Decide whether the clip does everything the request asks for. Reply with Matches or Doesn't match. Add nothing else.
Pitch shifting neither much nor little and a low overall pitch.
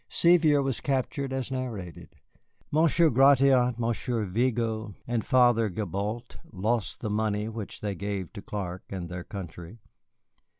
Matches